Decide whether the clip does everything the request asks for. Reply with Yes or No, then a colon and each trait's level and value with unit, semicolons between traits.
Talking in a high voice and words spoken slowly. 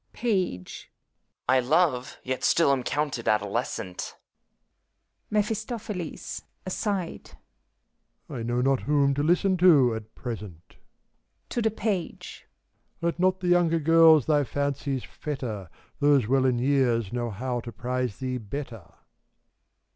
No: low, 135 Hz; slow, 125 wpm